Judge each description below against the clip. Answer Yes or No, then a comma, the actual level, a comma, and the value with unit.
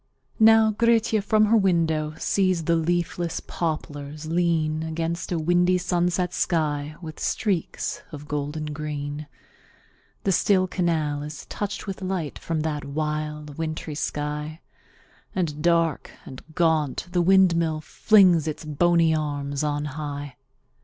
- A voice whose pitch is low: No, medium, 160 Hz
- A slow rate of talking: Yes, slow, 125 wpm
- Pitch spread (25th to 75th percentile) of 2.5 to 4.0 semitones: Yes, average, 2.9 semitones